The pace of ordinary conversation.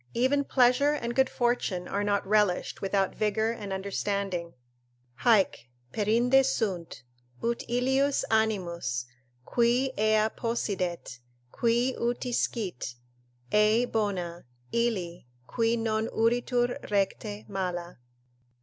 No: slow, 105 wpm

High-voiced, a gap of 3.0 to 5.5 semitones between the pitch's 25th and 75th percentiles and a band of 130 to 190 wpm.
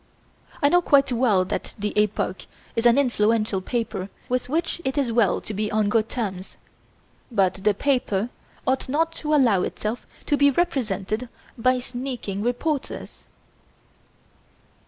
Yes: high, 235 Hz; average, 4.1 semitones; average, 140 wpm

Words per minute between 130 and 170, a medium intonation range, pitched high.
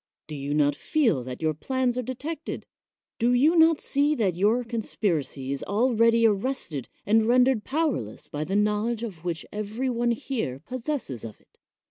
No: average, 160 wpm; wide, 7.8 semitones; high, 225 Hz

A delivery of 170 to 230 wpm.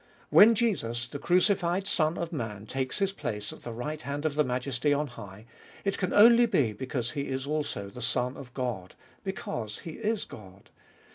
Yes: average, 190 wpm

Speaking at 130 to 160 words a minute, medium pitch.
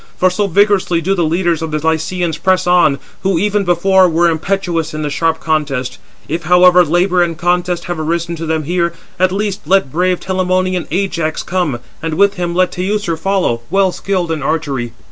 No: average, 185 wpm; medium, 175 Hz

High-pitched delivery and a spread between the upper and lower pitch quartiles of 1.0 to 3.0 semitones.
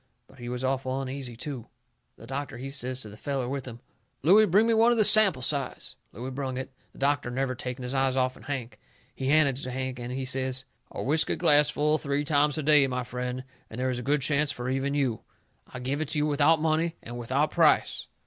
No: low, 135 Hz; narrow, 2.6 semitones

